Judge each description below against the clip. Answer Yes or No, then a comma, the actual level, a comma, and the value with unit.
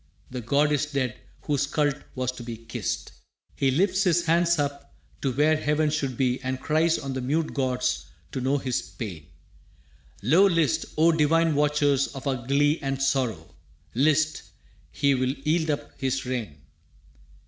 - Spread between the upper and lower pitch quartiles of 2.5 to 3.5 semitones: Yes, average, 3.0 semitones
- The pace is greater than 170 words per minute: No, average, 160 wpm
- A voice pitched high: No, medium, 140 Hz